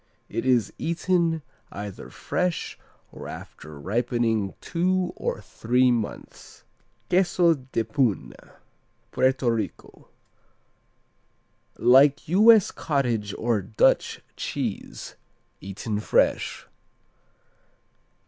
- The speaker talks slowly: Yes, slow, 80 wpm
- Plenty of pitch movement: Yes, wide, 7.1 semitones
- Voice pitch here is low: Yes, low, 125 Hz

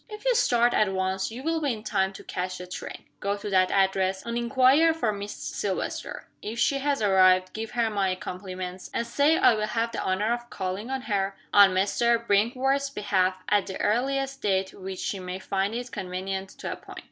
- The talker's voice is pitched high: Yes, high, 205 Hz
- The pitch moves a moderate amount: Yes, average, 4.1 semitones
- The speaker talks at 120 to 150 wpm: No, fast, 205 wpm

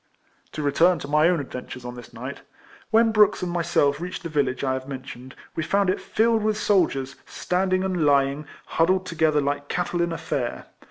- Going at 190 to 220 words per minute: Yes, average, 195 wpm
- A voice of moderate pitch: Yes, medium, 160 Hz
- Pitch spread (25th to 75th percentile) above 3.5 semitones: Yes, average, 5.0 semitones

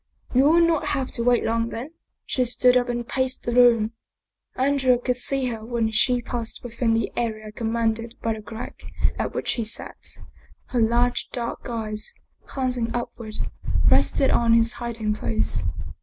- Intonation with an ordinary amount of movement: No, narrow, 1.8 semitones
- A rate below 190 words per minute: Yes, average, 170 wpm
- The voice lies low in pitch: No, high, 235 Hz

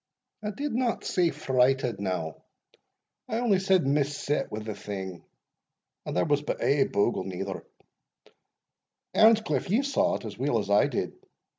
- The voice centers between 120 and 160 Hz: Yes, medium, 140 Hz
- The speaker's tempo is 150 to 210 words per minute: Yes, average, 155 wpm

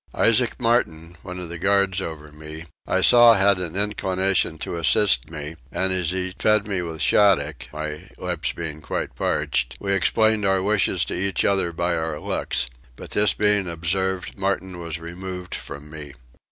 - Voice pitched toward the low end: Yes, very low, 90 Hz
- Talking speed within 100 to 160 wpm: No, average, 170 wpm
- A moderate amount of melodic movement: Yes, average, 3.4 semitones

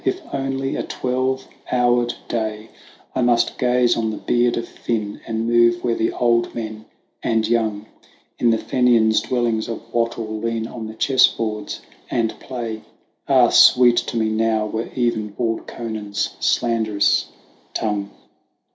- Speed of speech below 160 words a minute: Yes, average, 145 wpm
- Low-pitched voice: Yes, low, 115 Hz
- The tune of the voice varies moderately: No, narrow, 1.8 semitones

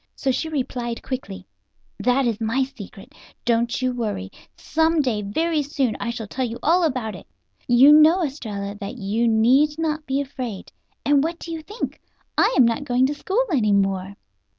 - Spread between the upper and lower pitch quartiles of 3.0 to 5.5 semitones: Yes, average, 5.1 semitones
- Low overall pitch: No, very high, 255 Hz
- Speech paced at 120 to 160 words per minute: No, average, 185 wpm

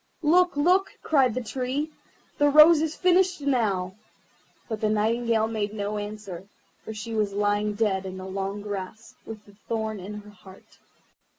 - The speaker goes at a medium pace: Yes, average, 165 wpm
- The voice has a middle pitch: No, high, 215 Hz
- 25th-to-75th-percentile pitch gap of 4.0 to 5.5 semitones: Yes, average, 4.6 semitones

